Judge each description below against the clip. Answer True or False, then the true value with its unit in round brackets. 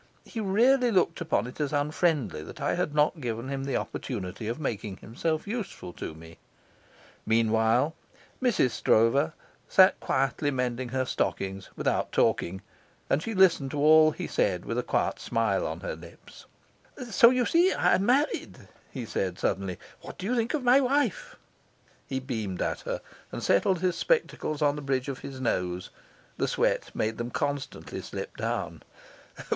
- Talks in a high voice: False (145 Hz)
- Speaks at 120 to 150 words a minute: False (165 wpm)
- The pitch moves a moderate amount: False (8.7 semitones)